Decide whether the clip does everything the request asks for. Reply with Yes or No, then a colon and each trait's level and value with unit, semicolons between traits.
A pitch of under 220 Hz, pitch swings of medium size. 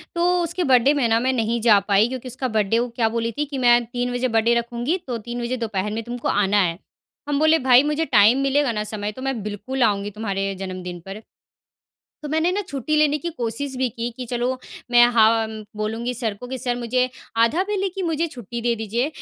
No: high, 240 Hz; average, 3.2 semitones